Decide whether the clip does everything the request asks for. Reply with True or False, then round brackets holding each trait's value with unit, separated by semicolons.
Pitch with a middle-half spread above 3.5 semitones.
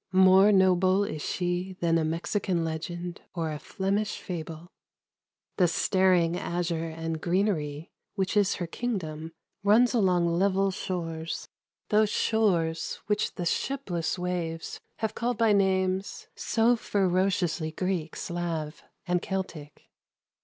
False (2.9 semitones)